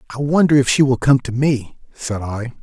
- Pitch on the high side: No, low, 130 Hz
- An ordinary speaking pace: No, fast, 230 wpm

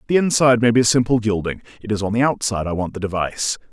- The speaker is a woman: No, male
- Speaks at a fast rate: Yes, fast, 240 wpm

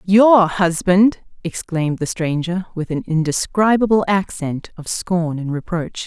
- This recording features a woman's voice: Yes, female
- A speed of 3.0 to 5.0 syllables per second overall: Yes, 4.1 syllables/s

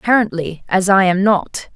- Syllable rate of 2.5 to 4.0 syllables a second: No, 4.8 syllables/s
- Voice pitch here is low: No, high, 190 Hz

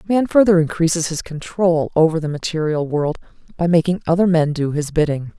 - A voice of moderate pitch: Yes, medium, 165 Hz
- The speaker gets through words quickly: No, average, 180 wpm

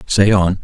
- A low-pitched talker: Yes, very low, 95 Hz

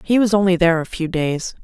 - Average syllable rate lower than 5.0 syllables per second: No, 6.1 syllables/s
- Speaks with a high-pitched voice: No, medium, 180 Hz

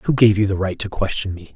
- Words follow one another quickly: Yes, fast, 310 wpm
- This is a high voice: No, low, 100 Hz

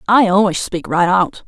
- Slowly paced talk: No, fast, 205 wpm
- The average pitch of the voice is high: Yes, high, 195 Hz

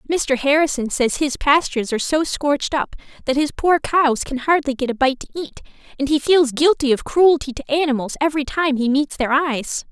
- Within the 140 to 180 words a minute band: No, fast, 205 wpm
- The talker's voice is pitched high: Yes, very high, 280 Hz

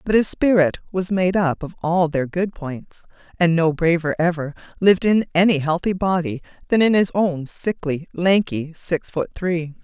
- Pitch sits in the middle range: Yes, medium, 170 Hz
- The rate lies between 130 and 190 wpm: Yes, average, 175 wpm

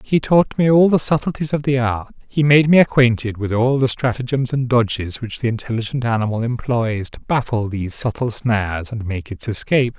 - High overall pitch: No, low, 120 Hz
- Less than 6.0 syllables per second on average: Yes, 5.3 syllables/s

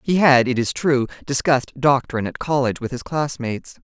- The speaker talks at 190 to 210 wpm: Yes, average, 200 wpm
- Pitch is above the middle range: No, low, 135 Hz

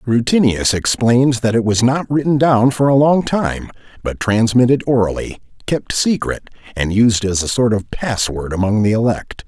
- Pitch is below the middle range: Yes, low, 120 Hz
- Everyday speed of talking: Yes, average, 170 wpm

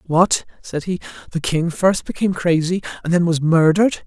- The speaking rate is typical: Yes, average, 175 wpm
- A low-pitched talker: No, medium, 170 Hz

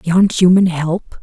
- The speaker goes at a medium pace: Yes, average, 145 wpm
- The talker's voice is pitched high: No, medium, 175 Hz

